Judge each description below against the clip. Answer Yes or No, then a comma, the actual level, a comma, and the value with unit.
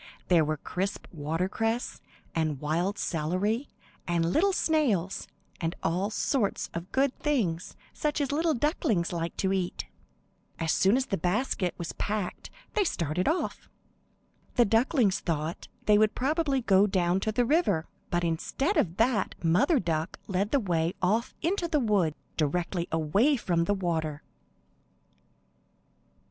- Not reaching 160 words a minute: Yes, average, 140 wpm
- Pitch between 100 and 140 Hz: No, high, 195 Hz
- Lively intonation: Yes, wide, 6.8 semitones